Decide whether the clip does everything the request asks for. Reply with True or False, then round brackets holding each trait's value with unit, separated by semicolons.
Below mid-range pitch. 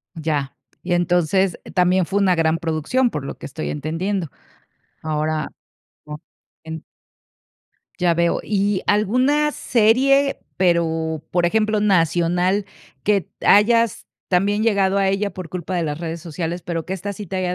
False (180 Hz)